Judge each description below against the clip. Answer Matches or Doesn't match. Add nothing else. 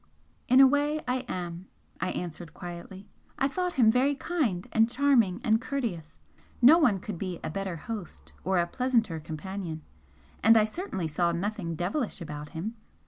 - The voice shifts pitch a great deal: Matches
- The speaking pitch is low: Doesn't match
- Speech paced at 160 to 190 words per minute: Matches